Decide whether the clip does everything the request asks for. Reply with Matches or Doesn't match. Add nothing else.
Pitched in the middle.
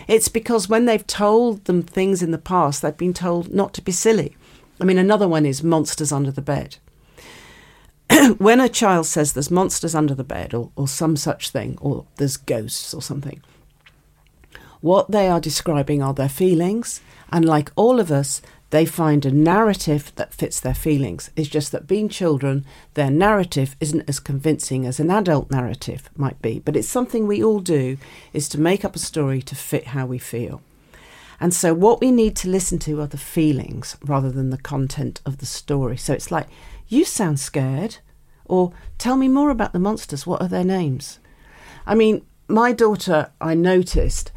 Matches